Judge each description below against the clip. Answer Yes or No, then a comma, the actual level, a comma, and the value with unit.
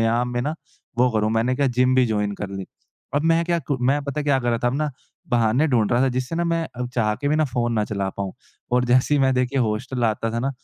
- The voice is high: No, low, 125 Hz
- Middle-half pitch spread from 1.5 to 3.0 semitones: No, average, 3.7 semitones